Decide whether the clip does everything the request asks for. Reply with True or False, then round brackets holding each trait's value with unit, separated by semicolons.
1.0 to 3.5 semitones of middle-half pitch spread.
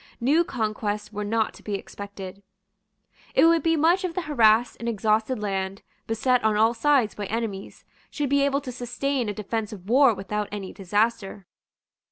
False (4.3 semitones)